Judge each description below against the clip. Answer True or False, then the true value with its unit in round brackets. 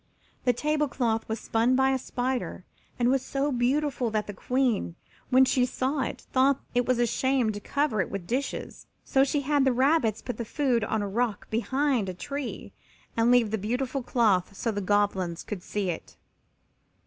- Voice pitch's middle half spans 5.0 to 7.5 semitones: False (3.8 semitones)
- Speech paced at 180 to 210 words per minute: True (190 wpm)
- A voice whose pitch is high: True (245 Hz)